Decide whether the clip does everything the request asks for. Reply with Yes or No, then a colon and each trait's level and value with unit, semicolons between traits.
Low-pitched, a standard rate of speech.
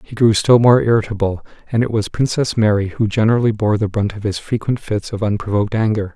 No: low, 110 Hz; fast, 215 wpm